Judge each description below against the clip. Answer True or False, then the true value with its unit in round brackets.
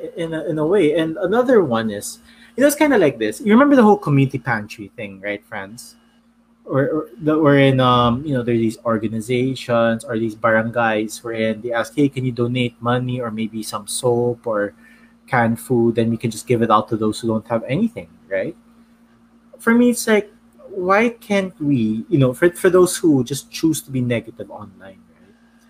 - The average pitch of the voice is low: True (130 Hz)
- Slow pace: False (205 wpm)